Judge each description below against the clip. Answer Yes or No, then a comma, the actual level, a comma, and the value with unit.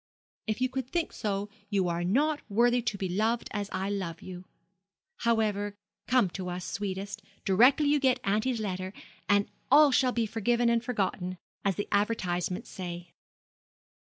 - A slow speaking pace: No, average, 155 wpm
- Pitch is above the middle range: Yes, high, 205 Hz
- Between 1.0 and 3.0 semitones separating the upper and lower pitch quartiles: No, average, 4.2 semitones